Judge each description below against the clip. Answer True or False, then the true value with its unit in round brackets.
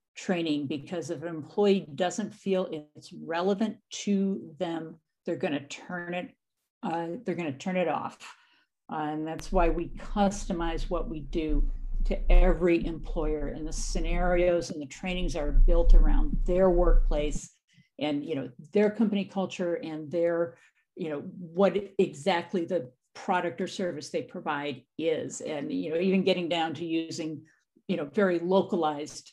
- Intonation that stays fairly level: False (3.1 semitones)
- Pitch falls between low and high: True (170 Hz)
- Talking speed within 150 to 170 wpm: True (160 wpm)